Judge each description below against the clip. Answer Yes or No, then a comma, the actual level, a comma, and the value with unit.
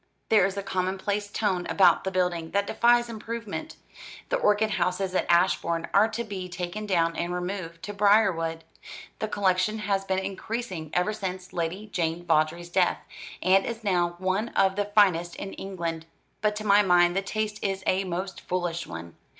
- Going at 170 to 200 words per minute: Yes, average, 175 wpm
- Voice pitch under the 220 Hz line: Yes, high, 190 Hz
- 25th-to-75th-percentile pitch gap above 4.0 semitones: No, average, 2.9 semitones